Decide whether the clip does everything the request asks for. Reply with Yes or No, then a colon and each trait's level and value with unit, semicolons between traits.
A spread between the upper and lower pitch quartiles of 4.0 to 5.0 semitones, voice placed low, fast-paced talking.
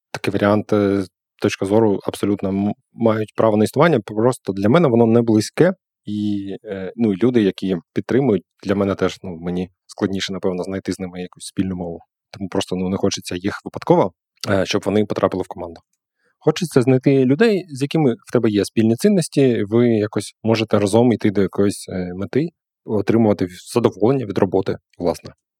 No: average, 3.3 semitones; low, 105 Hz; fast, 160 wpm